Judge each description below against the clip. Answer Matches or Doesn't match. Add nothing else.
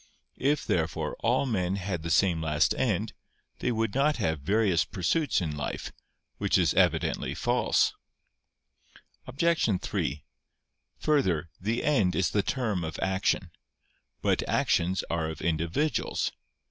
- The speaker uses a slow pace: Matches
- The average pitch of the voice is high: Doesn't match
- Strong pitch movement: Matches